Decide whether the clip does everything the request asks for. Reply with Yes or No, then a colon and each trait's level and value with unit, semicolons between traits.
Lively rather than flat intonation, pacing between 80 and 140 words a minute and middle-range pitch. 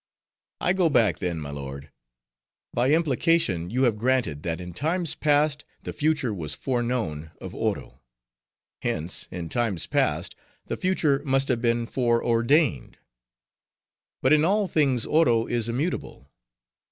No: wide, 8.9 semitones; slow, 135 wpm; low, 120 Hz